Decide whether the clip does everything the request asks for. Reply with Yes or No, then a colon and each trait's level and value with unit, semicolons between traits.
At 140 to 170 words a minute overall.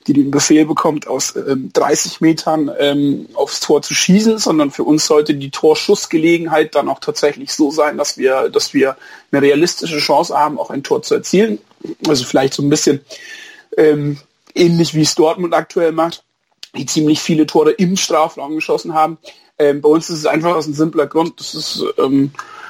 No: average, 185 wpm